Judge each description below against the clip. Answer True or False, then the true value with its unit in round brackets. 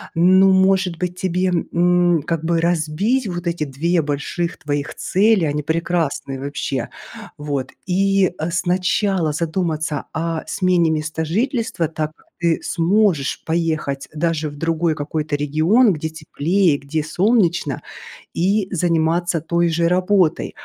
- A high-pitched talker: False (170 Hz)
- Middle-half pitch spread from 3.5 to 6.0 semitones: False (2.9 semitones)